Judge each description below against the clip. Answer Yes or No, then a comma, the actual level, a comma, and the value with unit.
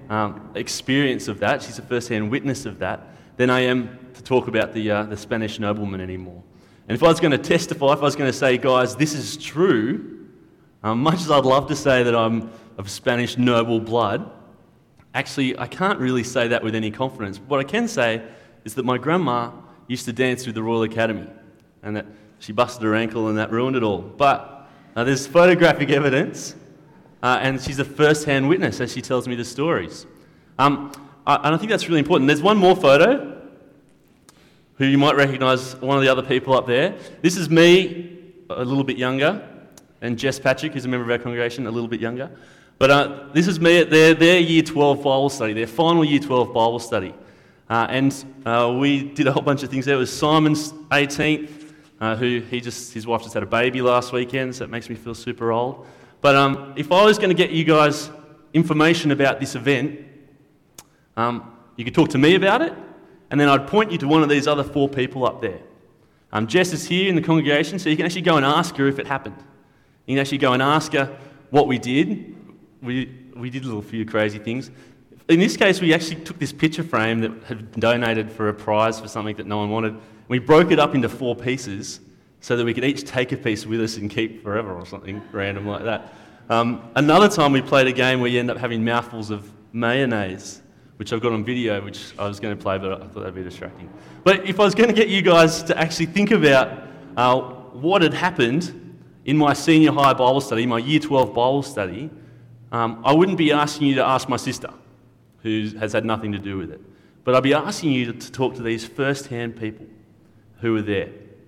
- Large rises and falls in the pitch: No, average, 4.3 semitones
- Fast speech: Yes, fast, 220 wpm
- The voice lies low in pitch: Yes, low, 130 Hz